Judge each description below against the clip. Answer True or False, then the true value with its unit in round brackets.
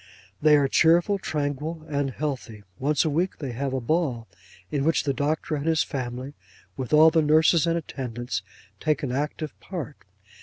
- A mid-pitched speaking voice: True (150 Hz)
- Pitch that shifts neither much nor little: True (3.0 semitones)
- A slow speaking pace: False (175 wpm)